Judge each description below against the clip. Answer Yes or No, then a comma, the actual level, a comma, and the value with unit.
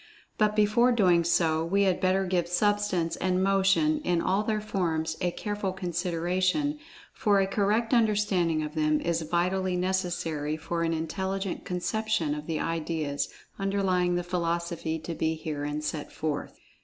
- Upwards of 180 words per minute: No, average, 150 wpm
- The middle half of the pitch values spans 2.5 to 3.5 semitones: Yes, average, 3.2 semitones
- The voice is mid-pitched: Yes, medium, 180 Hz